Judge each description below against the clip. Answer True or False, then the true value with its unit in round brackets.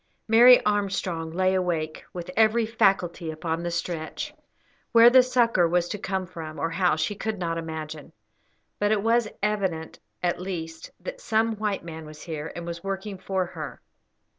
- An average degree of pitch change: True (4.3 semitones)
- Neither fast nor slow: True (165 wpm)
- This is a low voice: False (180 Hz)